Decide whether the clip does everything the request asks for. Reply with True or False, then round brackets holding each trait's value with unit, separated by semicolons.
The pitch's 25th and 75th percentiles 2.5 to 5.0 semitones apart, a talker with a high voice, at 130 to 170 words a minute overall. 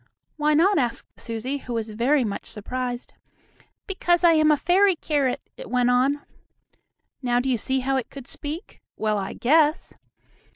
True (4.2 semitones; 265 Hz; 165 wpm)